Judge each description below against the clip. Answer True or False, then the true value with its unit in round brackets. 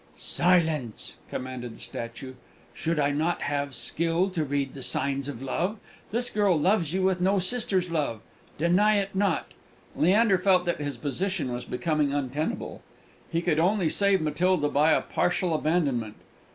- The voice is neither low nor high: True (165 Hz)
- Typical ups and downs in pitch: True (4.7 semitones)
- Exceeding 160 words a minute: False (155 wpm)